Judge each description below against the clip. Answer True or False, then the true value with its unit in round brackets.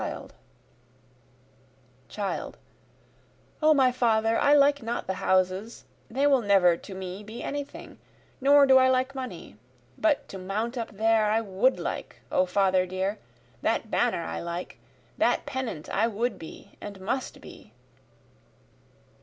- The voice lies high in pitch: True (220 Hz)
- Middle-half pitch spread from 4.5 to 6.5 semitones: True (5.5 semitones)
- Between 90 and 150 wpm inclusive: True (140 wpm)